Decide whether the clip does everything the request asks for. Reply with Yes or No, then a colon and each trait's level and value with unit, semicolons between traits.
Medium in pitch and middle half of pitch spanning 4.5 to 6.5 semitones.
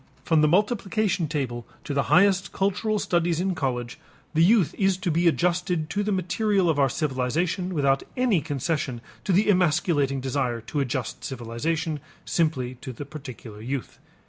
Yes: medium, 160 Hz; average, 5.3 semitones